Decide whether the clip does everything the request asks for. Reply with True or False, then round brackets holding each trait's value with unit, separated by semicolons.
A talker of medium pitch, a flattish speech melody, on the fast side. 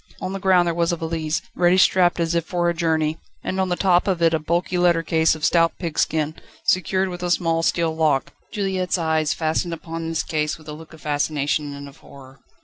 True (165 Hz; 2.0 semitones; 225 wpm)